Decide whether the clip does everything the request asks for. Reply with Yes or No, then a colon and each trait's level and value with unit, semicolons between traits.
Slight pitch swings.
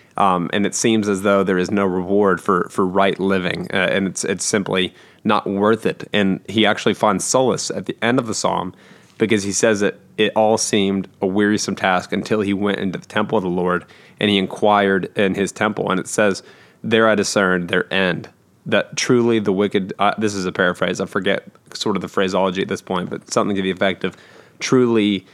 Yes: narrow, 2.2 semitones